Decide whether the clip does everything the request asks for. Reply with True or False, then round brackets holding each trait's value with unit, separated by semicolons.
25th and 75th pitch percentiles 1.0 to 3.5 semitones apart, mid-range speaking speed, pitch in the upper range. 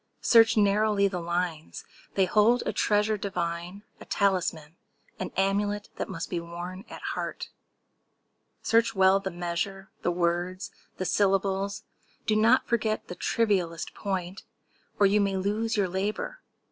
False (2.8 semitones; 125 wpm; 195 Hz)